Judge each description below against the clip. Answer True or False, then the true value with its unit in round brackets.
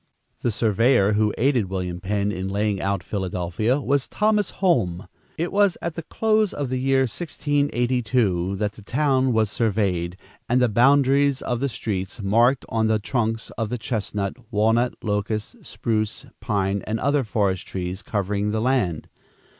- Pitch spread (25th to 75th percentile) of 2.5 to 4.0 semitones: False (4.8 semitones)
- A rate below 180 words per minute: True (155 wpm)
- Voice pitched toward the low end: True (110 Hz)